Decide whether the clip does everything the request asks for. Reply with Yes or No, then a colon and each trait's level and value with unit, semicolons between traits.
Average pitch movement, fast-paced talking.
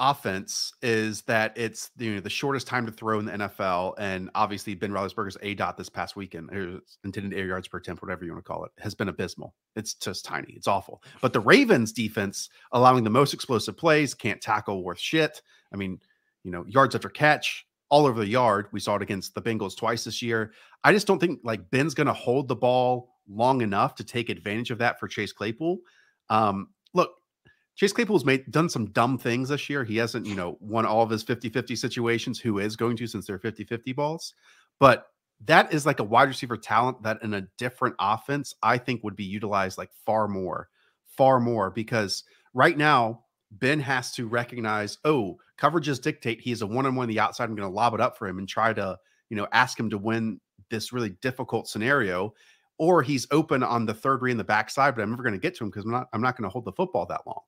Yes: average, 3.7 semitones; fast, 230 wpm